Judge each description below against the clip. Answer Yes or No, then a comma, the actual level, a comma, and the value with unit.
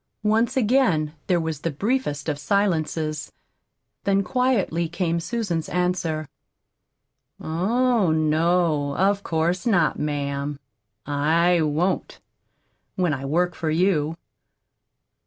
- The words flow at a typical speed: No, slow, 100 wpm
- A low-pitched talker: No, medium, 170 Hz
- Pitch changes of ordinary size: Yes, average, 4.2 semitones